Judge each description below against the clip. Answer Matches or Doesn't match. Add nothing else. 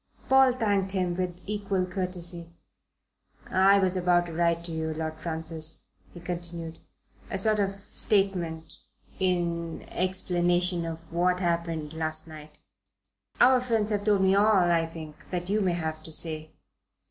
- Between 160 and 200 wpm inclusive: Doesn't match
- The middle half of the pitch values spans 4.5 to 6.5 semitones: Doesn't match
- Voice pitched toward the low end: Doesn't match